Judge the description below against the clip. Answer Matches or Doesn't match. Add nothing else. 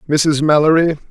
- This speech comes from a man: Matches